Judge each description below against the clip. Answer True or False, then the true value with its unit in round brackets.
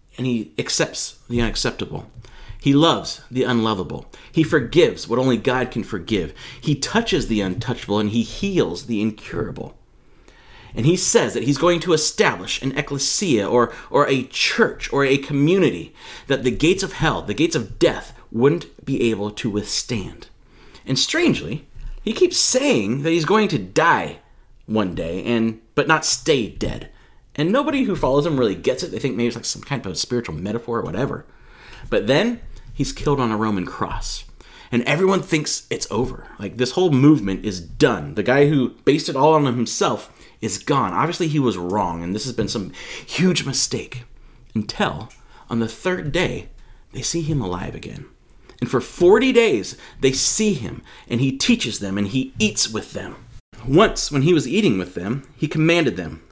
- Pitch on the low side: True (125 Hz)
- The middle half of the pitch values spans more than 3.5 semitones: True (5.6 semitones)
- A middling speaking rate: True (180 wpm)